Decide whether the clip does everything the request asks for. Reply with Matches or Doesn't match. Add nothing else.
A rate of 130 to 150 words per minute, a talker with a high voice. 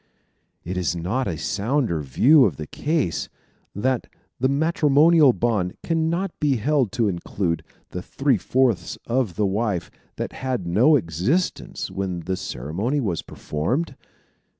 Doesn't match